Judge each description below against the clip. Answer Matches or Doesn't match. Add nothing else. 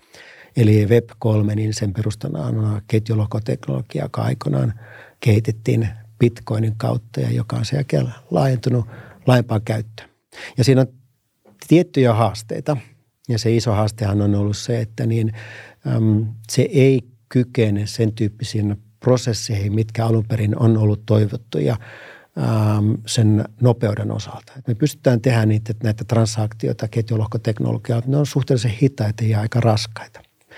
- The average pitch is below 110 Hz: Doesn't match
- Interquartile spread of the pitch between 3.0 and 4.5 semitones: Doesn't match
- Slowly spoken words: Doesn't match